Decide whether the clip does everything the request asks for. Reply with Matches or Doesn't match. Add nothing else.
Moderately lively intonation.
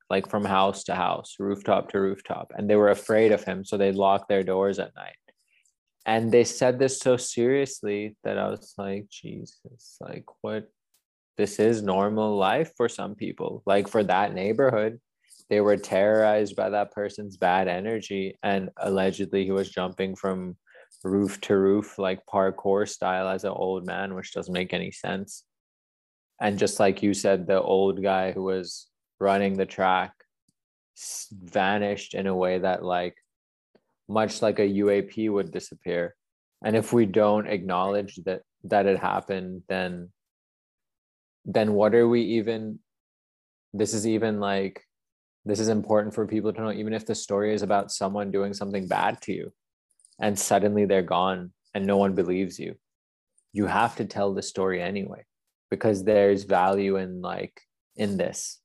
Doesn't match